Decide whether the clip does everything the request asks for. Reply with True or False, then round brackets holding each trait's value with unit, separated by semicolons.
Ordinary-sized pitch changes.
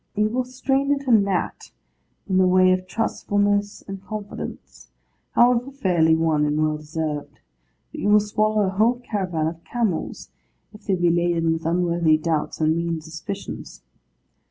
True (4.6 semitones)